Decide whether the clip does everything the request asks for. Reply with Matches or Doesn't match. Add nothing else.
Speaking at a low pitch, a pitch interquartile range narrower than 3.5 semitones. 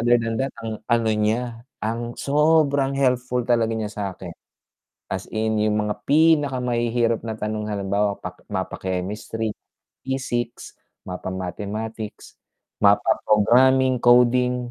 Matches